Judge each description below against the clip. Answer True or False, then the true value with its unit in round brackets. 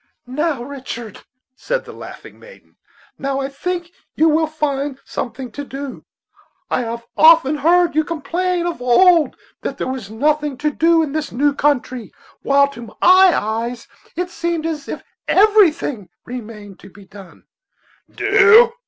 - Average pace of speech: True (150 wpm)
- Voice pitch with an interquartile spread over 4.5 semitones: True (5.3 semitones)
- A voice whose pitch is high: True (290 Hz)